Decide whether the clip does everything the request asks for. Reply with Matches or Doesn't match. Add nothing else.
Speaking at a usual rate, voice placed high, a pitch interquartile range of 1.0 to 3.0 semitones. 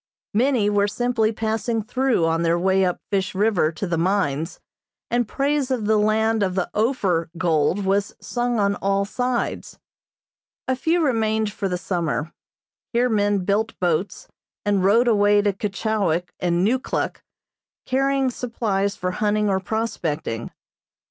Doesn't match